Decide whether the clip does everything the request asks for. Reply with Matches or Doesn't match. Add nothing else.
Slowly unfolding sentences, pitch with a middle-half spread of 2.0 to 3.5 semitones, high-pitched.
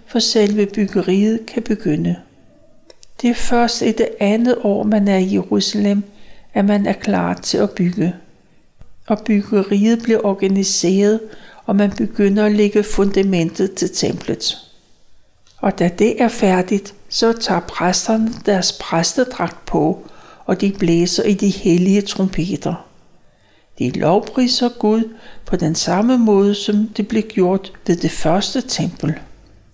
Matches